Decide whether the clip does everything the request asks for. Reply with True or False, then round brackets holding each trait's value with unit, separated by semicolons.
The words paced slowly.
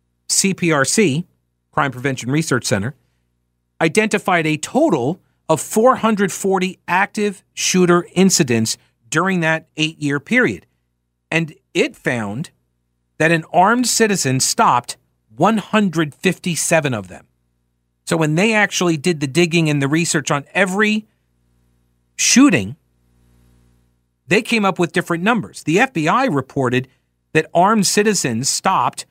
True (115 wpm)